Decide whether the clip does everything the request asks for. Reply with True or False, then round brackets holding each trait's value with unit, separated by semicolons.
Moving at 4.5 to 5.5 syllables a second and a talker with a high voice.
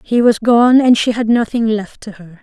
True (4.7 syllables/s; 225 Hz)